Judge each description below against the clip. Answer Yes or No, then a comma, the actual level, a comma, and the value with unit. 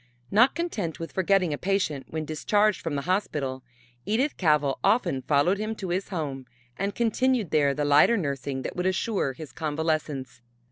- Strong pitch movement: Yes, wide, 5.8 semitones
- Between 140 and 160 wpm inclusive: No, average, 170 wpm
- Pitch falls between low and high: Yes, medium, 165 Hz